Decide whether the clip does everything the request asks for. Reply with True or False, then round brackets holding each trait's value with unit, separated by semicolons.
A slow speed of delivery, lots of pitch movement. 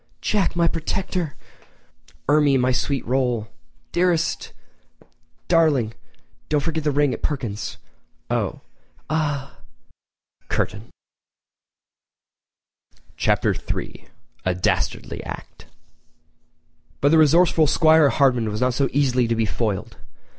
False (105 wpm; 4.7 semitones)